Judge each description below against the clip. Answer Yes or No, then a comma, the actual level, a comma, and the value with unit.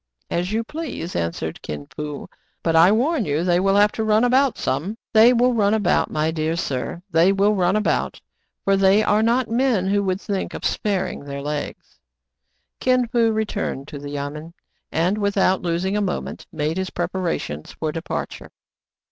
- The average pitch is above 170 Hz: Yes, high, 190 Hz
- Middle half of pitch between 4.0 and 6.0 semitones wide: Yes, average, 5.0 semitones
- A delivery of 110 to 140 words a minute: No, average, 180 wpm